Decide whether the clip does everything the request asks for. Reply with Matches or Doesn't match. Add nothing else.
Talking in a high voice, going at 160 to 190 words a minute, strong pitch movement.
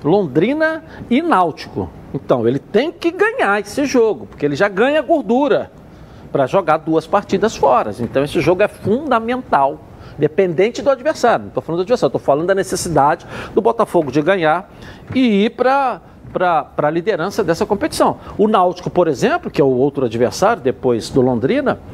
Matches